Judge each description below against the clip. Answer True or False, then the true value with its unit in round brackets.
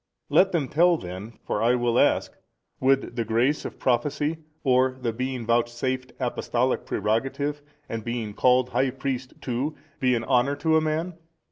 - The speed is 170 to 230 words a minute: False (160 wpm)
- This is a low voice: True (130 Hz)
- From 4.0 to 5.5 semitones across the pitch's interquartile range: False (3.2 semitones)